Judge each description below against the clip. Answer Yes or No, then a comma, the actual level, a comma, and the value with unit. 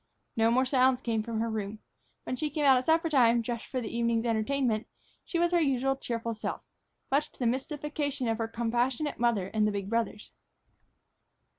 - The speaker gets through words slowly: No, average, 185 wpm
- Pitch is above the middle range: Yes, high, 240 Hz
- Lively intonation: No, average, 3.2 semitones